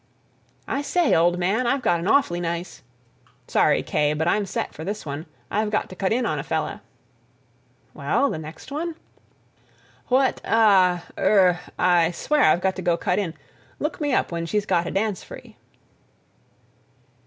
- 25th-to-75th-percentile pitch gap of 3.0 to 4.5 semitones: No, average, 4.9 semitones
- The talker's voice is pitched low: No, medium, 185 Hz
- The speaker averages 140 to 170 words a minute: Yes, average, 155 wpm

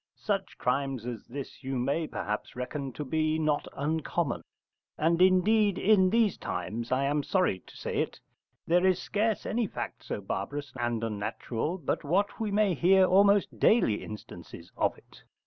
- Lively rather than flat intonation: Yes, wide, 7.0 semitones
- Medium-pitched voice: Yes, medium, 155 Hz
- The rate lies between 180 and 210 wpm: No, average, 165 wpm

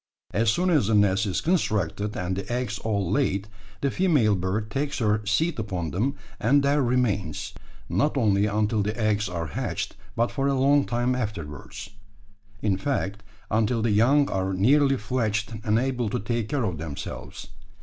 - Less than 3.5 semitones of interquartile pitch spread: No, average, 4.4 semitones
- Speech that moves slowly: No, average, 170 wpm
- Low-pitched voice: Yes, low, 110 Hz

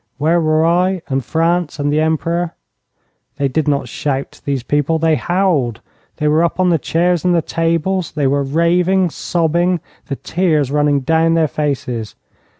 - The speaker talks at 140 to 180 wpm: Yes, average, 165 wpm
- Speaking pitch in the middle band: Yes, medium, 160 Hz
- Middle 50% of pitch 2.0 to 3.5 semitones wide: Yes, average, 2.9 semitones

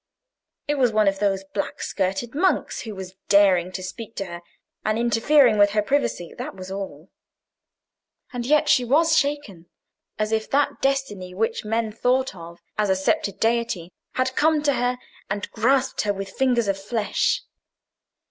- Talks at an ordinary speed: Yes, average, 165 wpm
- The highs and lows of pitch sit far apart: No, average, 4.9 semitones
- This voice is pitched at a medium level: No, high, 215 Hz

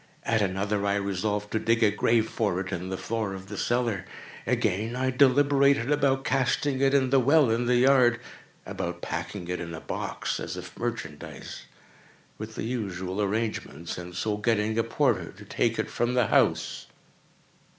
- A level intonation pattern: No, average, 4.3 semitones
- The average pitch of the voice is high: No, low, 110 Hz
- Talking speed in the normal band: Yes, average, 170 wpm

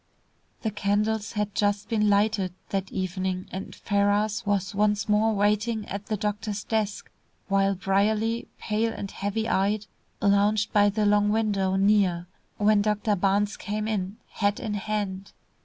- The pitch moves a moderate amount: No, narrow, 1.2 semitones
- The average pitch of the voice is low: No, high, 205 Hz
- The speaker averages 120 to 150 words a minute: Yes, average, 145 wpm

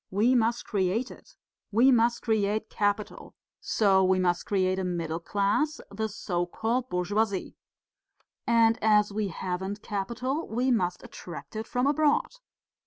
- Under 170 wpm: Yes, average, 140 wpm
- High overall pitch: Yes, high, 210 Hz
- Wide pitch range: No, average, 3.9 semitones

